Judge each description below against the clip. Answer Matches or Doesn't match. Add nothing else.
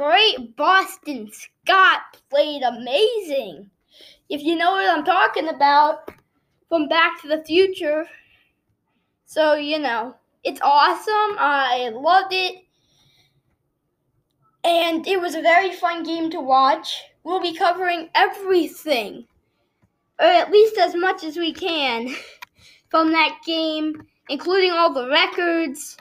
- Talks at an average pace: Doesn't match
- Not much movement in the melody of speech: Doesn't match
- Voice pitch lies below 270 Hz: Doesn't match